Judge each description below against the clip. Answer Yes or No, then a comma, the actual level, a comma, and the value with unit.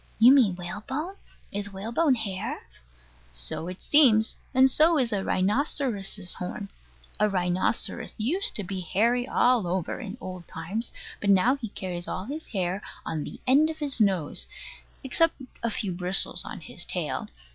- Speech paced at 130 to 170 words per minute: Yes, average, 155 wpm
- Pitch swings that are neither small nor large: No, wide, 5.7 semitones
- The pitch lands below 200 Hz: No, high, 210 Hz